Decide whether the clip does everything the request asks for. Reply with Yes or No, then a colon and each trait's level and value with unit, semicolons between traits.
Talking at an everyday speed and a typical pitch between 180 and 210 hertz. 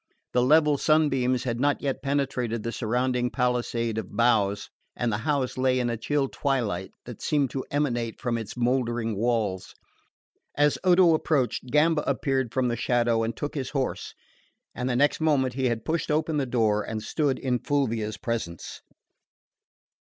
No: average, 165 wpm; low, 125 Hz